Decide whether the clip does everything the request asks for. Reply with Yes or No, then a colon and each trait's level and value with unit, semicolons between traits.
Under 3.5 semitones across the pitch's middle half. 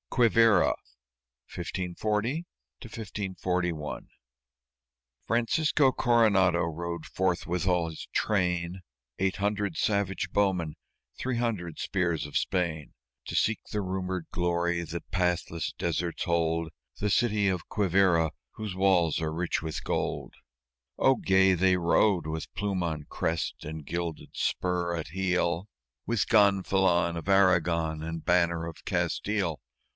Yes: average, 3.0 semitones